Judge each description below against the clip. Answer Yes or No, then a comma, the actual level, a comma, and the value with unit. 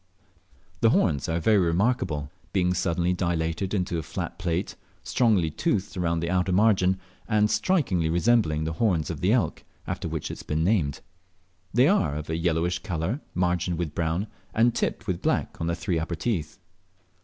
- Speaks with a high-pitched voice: No, very low, 90 Hz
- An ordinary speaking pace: Yes, average, 175 wpm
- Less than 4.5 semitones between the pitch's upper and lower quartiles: Yes, average, 3.6 semitones